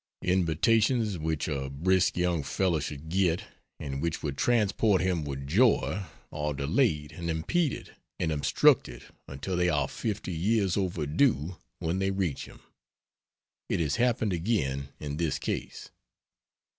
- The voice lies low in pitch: Yes, very low, 85 Hz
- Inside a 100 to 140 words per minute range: Yes, slow, 135 wpm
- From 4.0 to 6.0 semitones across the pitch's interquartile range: Yes, average, 4.6 semitones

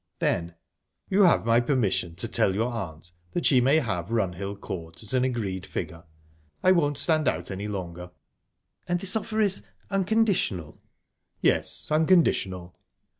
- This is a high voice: No, low, 115 Hz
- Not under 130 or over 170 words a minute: Yes, average, 140 wpm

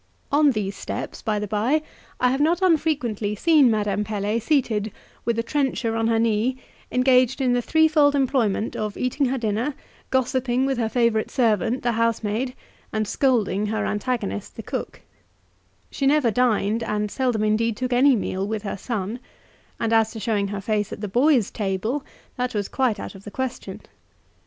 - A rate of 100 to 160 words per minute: No, average, 175 wpm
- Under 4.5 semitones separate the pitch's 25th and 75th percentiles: Yes, average, 3.7 semitones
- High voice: Yes, high, 230 Hz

